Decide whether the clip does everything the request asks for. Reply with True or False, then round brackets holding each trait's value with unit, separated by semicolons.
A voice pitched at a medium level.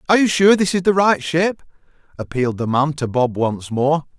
True (155 Hz)